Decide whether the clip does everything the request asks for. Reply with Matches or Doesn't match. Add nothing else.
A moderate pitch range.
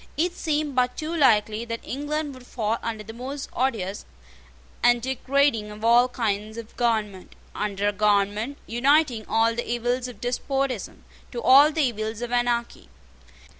Matches